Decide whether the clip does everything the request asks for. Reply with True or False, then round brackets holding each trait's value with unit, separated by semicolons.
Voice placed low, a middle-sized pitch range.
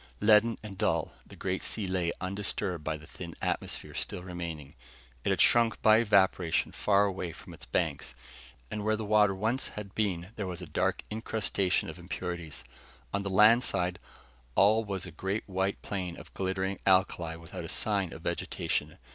True (95 Hz; 3.0 semitones)